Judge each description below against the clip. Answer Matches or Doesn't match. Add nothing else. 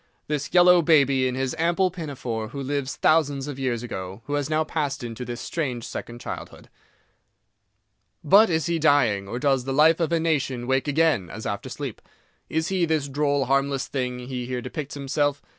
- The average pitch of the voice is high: Doesn't match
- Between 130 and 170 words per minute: Doesn't match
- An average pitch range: Matches